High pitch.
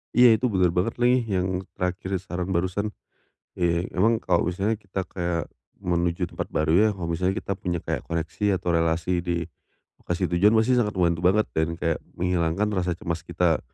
No: very low, 90 Hz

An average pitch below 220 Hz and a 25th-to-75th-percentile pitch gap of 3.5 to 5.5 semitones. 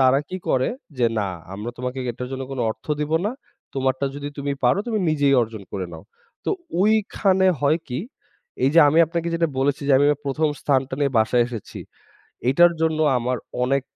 Yes: low, 135 Hz; average, 3.8 semitones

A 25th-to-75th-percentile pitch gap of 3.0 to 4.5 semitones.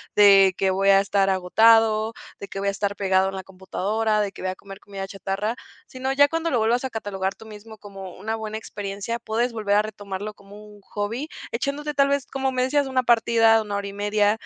No: narrow, 2.6 semitones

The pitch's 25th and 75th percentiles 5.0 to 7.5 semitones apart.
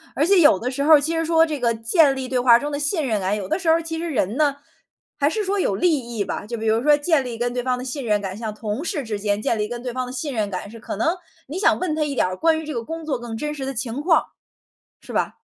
Yes: wide, 5.6 semitones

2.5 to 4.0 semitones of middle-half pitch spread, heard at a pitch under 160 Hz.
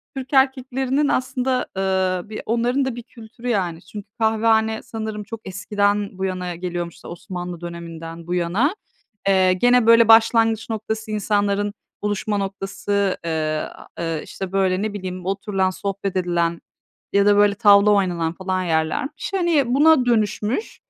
No: average, 3.6 semitones; high, 205 Hz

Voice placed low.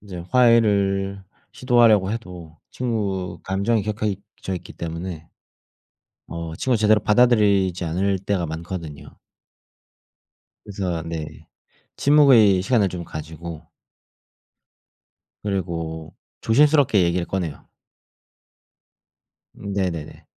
Yes: very low, 95 Hz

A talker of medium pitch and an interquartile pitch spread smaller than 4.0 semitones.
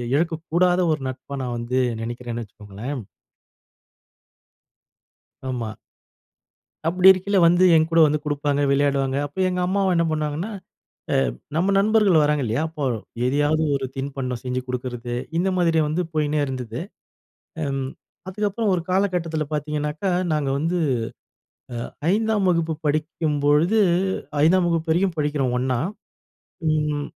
No: medium, 150 Hz; average, 4.5 semitones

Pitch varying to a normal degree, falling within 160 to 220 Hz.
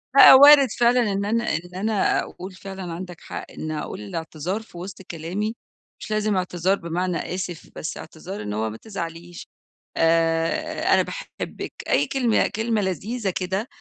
Yes: average, 4.4 semitones; medium, 185 Hz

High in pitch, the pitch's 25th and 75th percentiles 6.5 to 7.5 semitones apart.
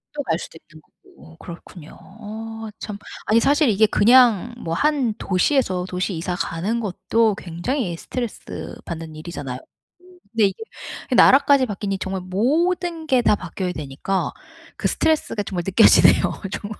No: high, 205 Hz; wide, 5.5 semitones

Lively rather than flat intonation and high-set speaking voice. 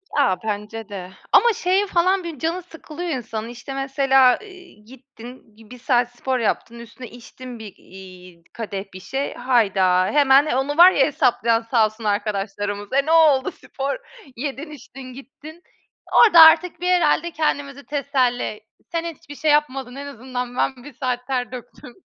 No: average, 4.7 semitones; very high, 255 Hz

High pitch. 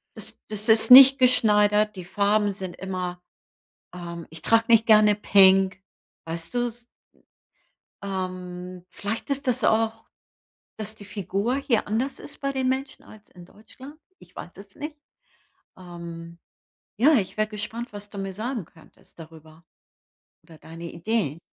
Yes: high, 205 Hz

